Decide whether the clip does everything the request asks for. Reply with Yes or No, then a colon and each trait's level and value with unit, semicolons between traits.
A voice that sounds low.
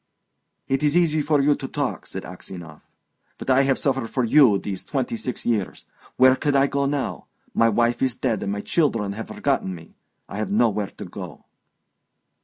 Yes: low, 125 Hz